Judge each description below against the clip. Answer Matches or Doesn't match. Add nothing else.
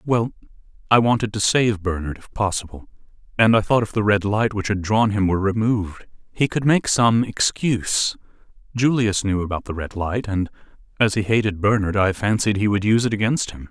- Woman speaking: Doesn't match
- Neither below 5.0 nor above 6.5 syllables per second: Matches